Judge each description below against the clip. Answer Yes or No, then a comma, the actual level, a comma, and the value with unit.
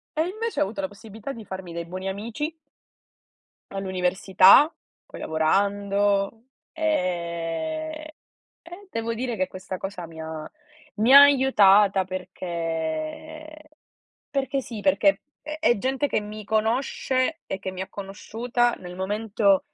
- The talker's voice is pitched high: Yes, high, 205 Hz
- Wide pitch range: Yes, wide, 6.3 semitones